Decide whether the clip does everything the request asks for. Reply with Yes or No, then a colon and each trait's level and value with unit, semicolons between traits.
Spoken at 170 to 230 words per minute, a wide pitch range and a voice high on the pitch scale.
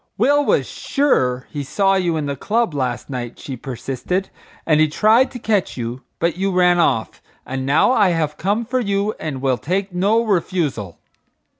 No: average, 180 wpm; wide, 7.1 semitones; medium, 175 Hz